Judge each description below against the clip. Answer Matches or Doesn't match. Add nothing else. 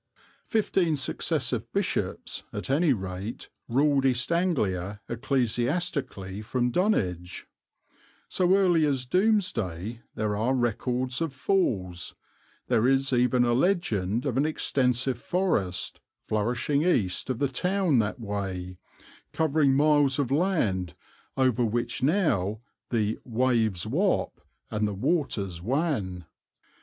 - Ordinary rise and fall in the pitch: Doesn't match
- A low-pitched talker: Matches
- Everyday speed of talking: Doesn't match